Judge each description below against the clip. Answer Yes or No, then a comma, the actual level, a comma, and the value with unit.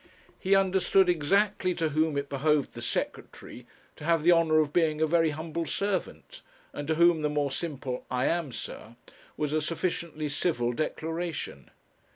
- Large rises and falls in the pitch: No, average, 2.8 semitones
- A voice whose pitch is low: No, medium, 155 Hz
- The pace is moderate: Yes, average, 165 wpm